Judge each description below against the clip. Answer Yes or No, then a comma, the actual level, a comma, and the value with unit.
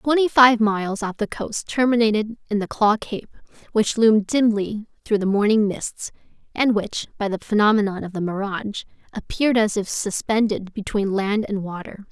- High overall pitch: Yes, high, 215 Hz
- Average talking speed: Yes, average, 170 wpm